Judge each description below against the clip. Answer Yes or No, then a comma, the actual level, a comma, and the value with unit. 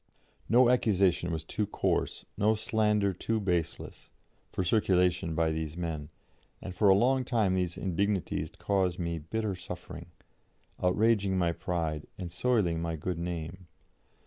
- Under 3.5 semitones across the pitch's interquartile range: No, average, 3.9 semitones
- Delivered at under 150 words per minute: Yes, average, 140 wpm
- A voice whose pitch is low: Yes, very low, 90 Hz